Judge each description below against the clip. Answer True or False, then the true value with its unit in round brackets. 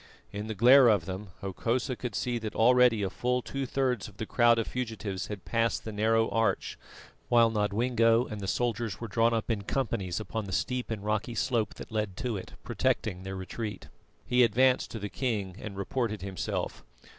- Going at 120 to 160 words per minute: False (190 wpm)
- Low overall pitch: True (110 Hz)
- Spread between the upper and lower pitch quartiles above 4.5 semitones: False (3.0 semitones)